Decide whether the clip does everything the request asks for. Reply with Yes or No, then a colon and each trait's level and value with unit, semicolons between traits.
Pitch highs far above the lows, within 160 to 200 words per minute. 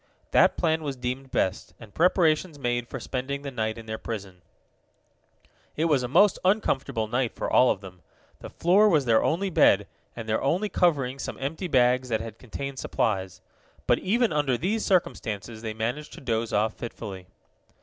Yes: wide, 6.0 semitones; average, 180 wpm